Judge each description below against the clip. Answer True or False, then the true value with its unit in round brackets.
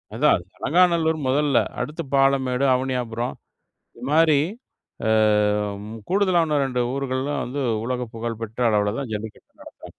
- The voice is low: True (130 Hz)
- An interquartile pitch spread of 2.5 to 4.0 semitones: False (4.9 semitones)